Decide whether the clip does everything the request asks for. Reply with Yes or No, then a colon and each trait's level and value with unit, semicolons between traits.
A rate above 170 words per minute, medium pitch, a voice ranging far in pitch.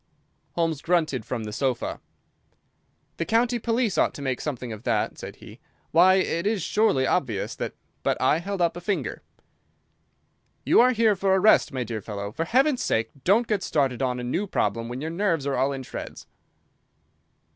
Yes: average, 190 wpm; medium, 160 Hz; wide, 8.0 semitones